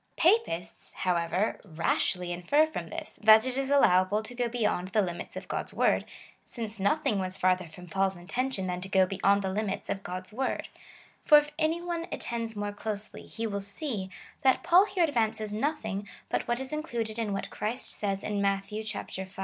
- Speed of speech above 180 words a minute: Yes, average, 190 wpm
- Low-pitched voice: No, high, 210 Hz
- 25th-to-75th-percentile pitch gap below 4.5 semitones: No, average, 5.3 semitones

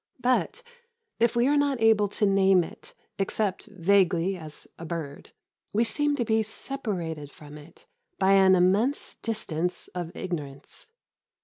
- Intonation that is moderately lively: Yes, average, 4.9 semitones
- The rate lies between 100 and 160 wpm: Yes, average, 140 wpm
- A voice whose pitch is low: No, high, 195 Hz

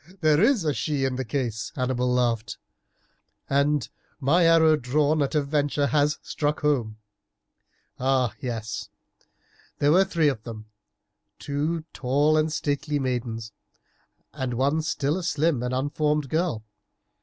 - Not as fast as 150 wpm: Yes, average, 140 wpm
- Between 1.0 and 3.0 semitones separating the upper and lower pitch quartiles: No, average, 3.4 semitones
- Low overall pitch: No, medium, 145 Hz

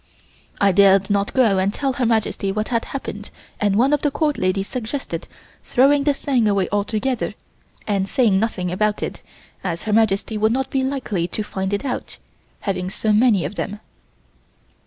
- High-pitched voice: Yes, high, 215 Hz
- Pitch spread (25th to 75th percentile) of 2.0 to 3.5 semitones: No, average, 4.3 semitones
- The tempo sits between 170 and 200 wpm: Yes, average, 180 wpm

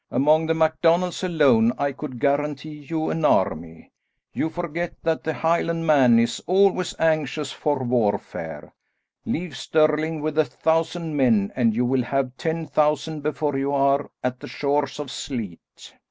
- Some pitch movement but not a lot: Yes, average, 3.8 semitones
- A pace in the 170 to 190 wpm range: No, average, 150 wpm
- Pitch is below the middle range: No, medium, 150 Hz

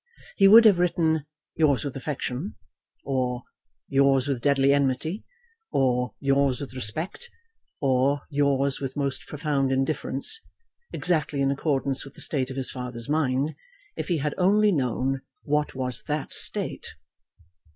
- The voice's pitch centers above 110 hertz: Yes, medium, 140 Hz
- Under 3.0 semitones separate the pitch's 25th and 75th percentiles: Yes, narrow, 2.5 semitones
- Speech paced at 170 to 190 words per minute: No, average, 140 wpm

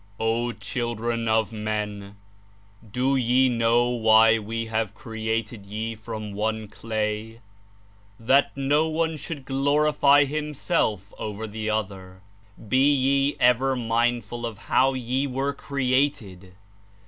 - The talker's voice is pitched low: Yes, low, 115 Hz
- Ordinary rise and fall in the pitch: Yes, average, 3.6 semitones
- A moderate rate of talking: No, slow, 115 wpm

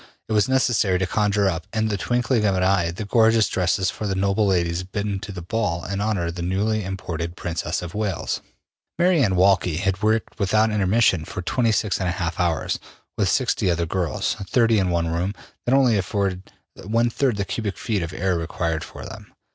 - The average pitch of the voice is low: Yes, low, 100 Hz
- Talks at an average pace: Yes, average, 195 wpm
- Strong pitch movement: No, average, 3.5 semitones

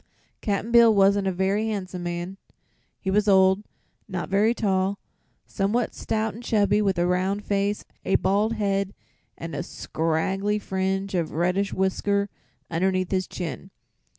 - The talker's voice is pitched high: Yes, high, 195 Hz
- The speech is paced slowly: No, average, 145 wpm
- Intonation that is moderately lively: No, narrow, 1.7 semitones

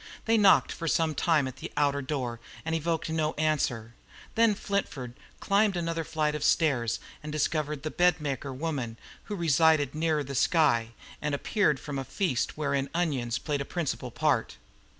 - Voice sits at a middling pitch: Yes, medium, 150 Hz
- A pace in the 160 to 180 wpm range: Yes, average, 170 wpm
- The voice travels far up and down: No, average, 3.4 semitones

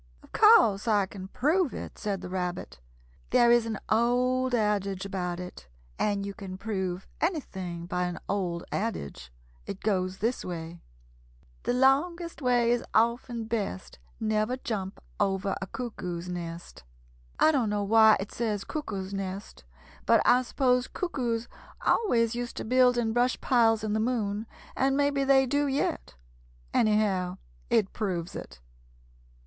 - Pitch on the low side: No, high, 215 Hz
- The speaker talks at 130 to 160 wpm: Yes, average, 150 wpm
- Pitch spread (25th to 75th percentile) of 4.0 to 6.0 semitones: Yes, average, 4.6 semitones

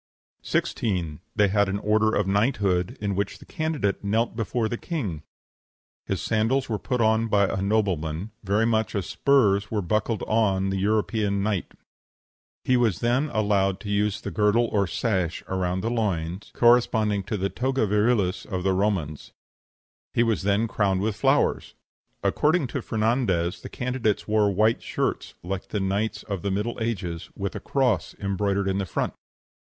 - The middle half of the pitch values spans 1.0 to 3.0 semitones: Yes, average, 2.7 semitones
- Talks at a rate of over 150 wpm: Yes, average, 165 wpm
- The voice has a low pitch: Yes, low, 105 Hz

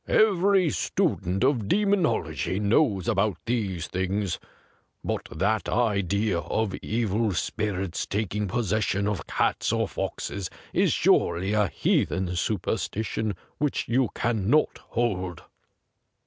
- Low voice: Yes, low, 105 Hz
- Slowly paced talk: Yes, slow, 115 wpm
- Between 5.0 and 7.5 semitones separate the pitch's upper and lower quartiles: No, average, 3.8 semitones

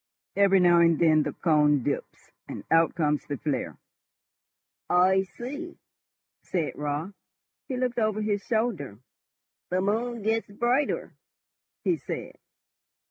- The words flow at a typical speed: No, slow, 125 wpm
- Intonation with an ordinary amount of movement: No, wide, 6.4 semitones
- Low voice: No, high, 190 Hz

